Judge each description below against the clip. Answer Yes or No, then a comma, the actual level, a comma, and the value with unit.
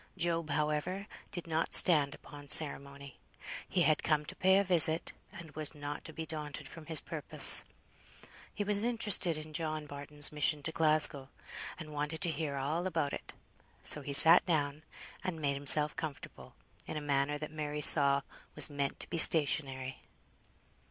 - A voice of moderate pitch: Yes, medium, 150 Hz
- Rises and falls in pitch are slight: Yes, narrow, 2.2 semitones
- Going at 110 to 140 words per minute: No, average, 165 wpm